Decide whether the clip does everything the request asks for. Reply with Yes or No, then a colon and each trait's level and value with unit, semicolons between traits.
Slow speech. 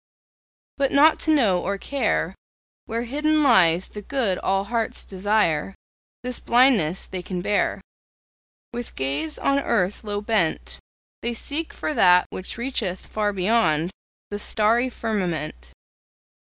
Yes: slow, 130 wpm